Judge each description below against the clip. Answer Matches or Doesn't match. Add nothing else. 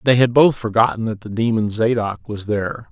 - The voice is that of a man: Matches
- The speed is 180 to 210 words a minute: Matches